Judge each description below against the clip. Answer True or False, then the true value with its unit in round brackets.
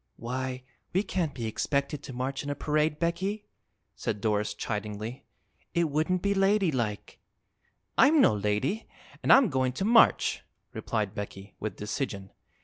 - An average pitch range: False (8.1 semitones)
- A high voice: False (135 Hz)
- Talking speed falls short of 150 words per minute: True (140 wpm)